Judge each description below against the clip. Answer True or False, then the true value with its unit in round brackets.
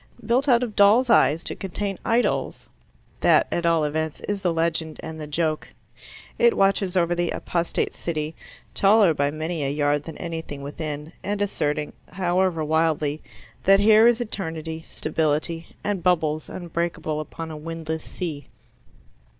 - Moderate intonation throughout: True (3.8 semitones)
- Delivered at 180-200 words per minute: False (150 wpm)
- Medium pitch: True (165 Hz)